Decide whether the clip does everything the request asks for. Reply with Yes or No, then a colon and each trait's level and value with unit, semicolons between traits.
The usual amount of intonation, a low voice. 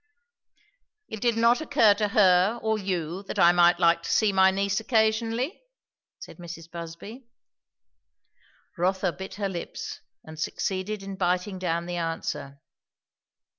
No: average, 3.8 semitones; high, 190 Hz